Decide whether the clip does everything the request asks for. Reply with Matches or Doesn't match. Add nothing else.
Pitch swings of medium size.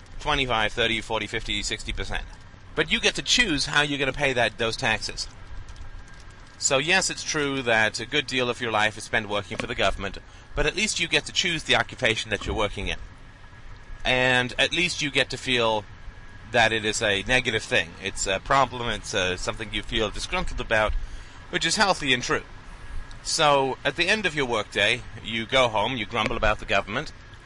Matches